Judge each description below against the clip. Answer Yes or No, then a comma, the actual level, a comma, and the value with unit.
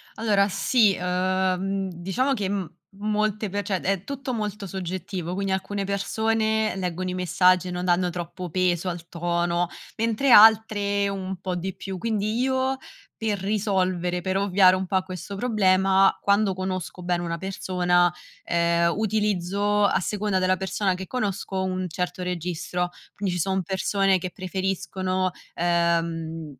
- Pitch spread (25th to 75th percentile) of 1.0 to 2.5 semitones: Yes, narrow, 2.2 semitones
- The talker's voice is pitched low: No, high, 190 Hz